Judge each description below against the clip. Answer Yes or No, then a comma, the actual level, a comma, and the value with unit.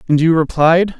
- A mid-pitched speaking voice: Yes, medium, 165 Hz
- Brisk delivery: No, average, 180 wpm